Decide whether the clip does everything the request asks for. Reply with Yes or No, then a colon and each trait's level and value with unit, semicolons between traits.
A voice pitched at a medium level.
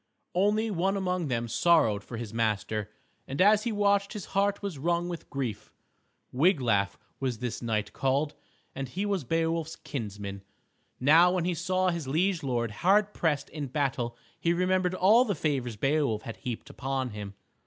Yes: medium, 150 Hz